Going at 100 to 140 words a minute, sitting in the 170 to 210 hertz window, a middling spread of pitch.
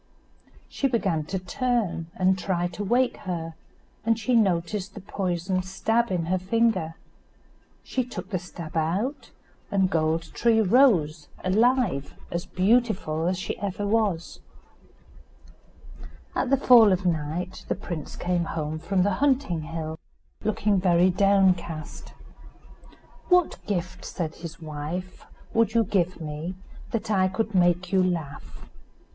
Yes: slow, 135 wpm; medium, 185 Hz; average, 4.3 semitones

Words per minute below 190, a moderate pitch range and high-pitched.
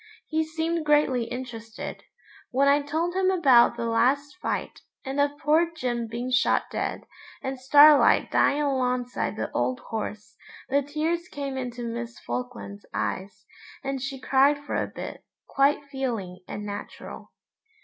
Yes: average, 145 wpm; average, 3.5 semitones; very high, 265 Hz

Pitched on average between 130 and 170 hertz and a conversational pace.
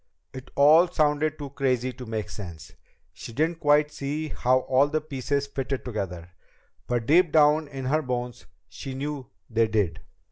Yes: low, 135 Hz; average, 165 wpm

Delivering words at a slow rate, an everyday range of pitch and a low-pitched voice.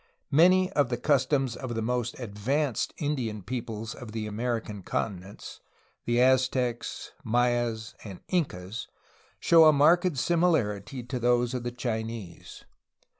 Yes: slow, 125 wpm; average, 3.6 semitones; low, 120 Hz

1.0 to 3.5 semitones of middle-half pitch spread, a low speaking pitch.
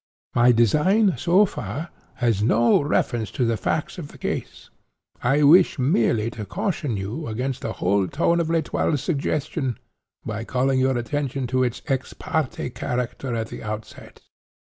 No: average, 4.7 semitones; low, 130 Hz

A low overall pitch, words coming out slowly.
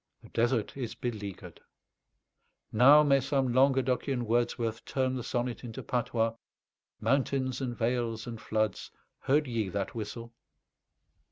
Yes: low, 120 Hz; slow, 120 wpm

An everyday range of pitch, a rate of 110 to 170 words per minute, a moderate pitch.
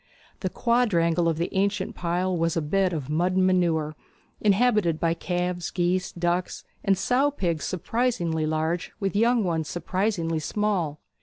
Yes: average, 3.0 semitones; average, 150 wpm; medium, 175 Hz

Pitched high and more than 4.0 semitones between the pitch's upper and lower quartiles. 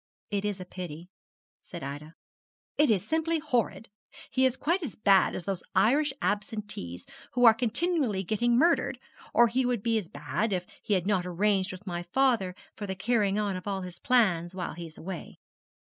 Yes: high, 205 Hz; average, 4.8 semitones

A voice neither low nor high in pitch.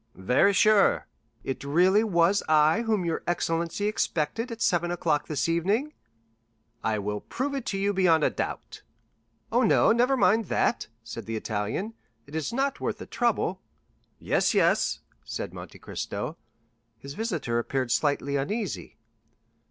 Yes: medium, 175 Hz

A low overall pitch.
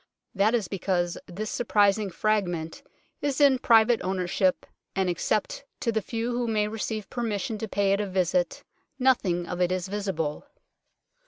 No: high, 205 Hz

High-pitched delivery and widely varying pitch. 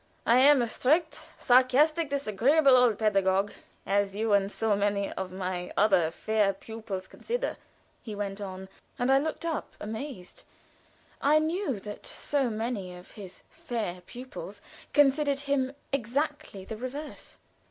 Yes: high, 230 Hz; wide, 6.0 semitones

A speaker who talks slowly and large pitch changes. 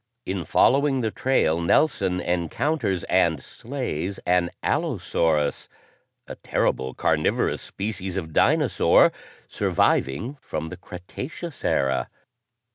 Yes: slow, 100 wpm; wide, 7.4 semitones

